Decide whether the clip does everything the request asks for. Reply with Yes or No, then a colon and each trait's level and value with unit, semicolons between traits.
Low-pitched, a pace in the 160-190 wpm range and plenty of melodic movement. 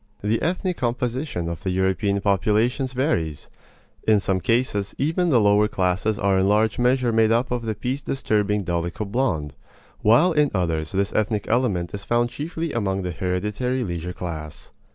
No: low, 105 Hz; average, 165 wpm; average, 4.8 semitones